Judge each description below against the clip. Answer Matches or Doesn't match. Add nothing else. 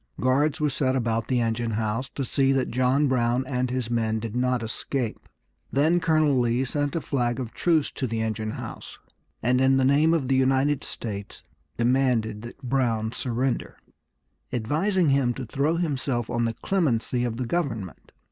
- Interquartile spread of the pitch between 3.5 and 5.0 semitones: Doesn't match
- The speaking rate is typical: Matches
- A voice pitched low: Matches